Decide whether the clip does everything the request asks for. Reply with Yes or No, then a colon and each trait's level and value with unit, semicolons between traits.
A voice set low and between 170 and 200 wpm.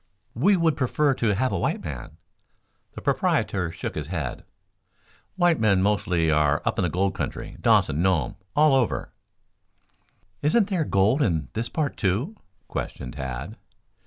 No: low, 100 Hz; average, 150 wpm